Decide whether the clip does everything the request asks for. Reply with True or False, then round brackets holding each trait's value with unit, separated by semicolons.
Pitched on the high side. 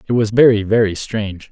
False (110 Hz)